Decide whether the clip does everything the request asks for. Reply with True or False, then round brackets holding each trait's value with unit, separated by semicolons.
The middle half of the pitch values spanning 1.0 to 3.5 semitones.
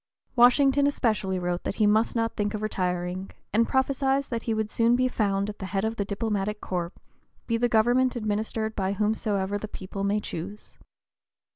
True (2.8 semitones)